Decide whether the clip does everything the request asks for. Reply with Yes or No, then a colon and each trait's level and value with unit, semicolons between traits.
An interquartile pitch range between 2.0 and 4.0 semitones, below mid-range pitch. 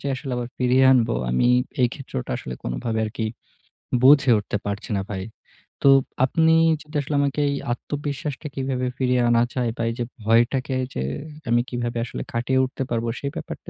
Yes: average, 2.8 semitones; low, 125 Hz